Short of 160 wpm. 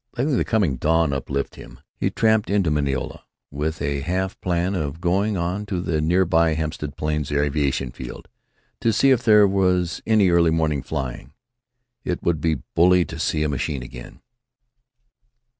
No: average, 165 wpm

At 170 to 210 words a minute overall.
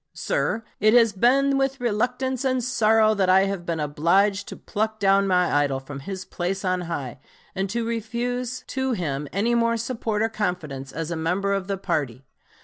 Yes: average, 185 wpm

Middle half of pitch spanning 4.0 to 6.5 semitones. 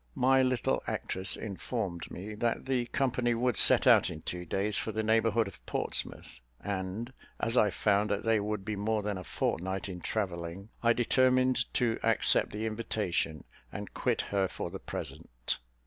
No: average, 3.6 semitones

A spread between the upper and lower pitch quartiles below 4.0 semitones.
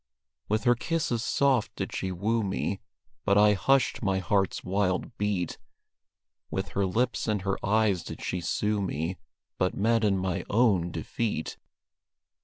Yes: average, 3.3 semitones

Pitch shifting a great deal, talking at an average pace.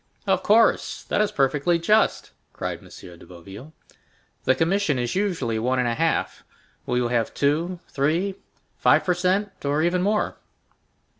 Yes: wide, 6.9 semitones; average, 145 wpm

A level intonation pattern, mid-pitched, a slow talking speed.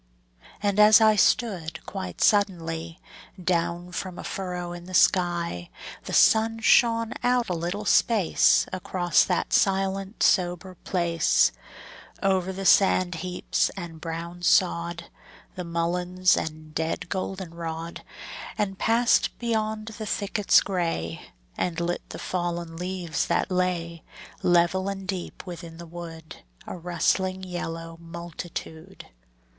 Yes: narrow, 2.3 semitones; medium, 180 Hz; slow, 120 wpm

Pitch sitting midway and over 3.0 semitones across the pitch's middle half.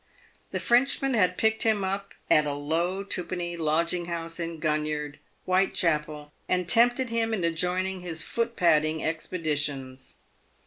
Yes: medium, 170 Hz; average, 3.9 semitones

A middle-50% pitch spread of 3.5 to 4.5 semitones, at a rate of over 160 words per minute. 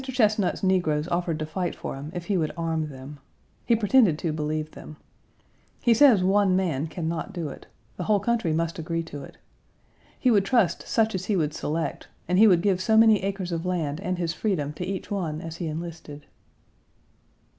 Yes: average, 4.1 semitones; average, 200 wpm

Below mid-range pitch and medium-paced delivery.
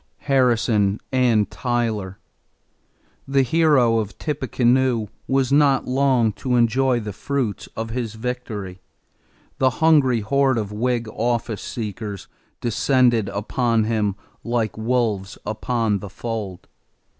No: low, 120 Hz; slow, 110 wpm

